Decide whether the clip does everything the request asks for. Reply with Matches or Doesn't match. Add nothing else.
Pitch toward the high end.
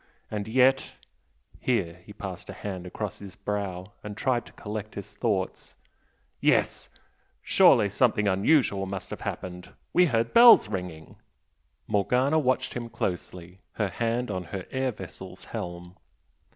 Doesn't match